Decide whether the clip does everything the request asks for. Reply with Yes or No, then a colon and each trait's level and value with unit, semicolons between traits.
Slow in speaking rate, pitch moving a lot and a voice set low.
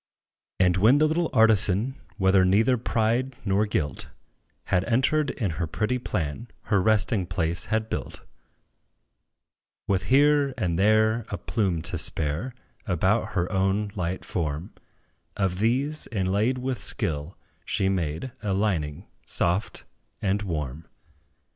No: slow, 130 wpm; average, 4.4 semitones; low, 100 Hz